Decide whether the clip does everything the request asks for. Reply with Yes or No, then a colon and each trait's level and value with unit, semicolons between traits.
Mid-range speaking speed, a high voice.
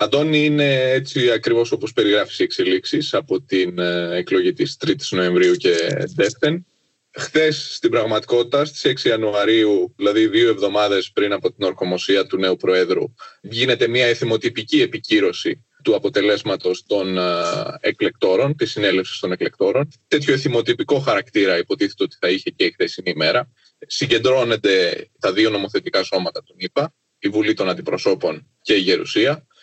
Yes: average, 140 wpm; very high, 345 Hz